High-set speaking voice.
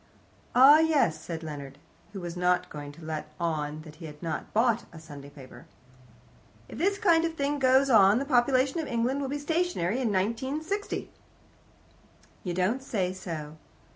Yes: high, 210 Hz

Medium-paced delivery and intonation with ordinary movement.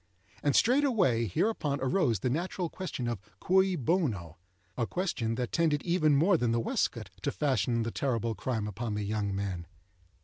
No: average, 160 wpm; wide, 7.7 semitones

